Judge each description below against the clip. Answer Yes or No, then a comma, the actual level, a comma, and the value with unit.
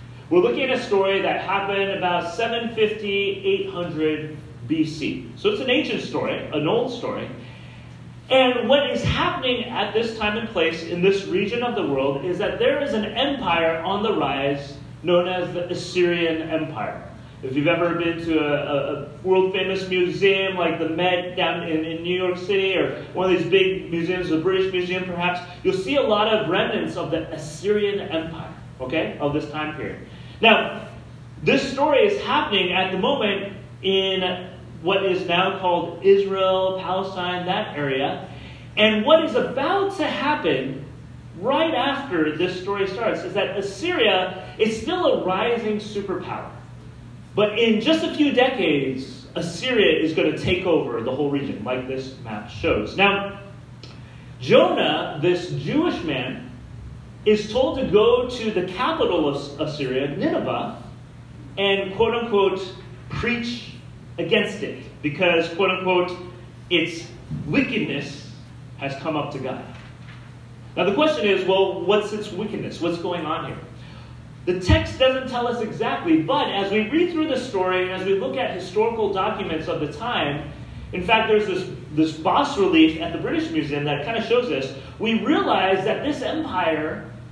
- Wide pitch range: Yes, wide, 5.7 semitones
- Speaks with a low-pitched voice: No, medium, 180 Hz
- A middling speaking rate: Yes, average, 160 wpm